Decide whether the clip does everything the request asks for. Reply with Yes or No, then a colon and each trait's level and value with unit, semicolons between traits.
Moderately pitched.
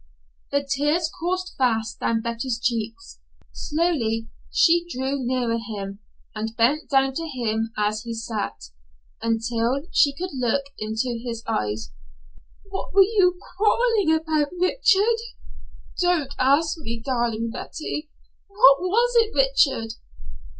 No: very high, 270 Hz